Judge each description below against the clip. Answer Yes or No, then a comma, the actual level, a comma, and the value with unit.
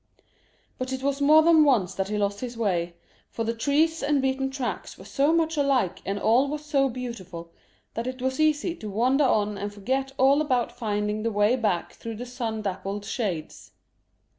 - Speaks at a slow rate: No, average, 190 wpm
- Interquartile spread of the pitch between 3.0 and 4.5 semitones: No, average, 5.1 semitones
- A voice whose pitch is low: No, high, 245 Hz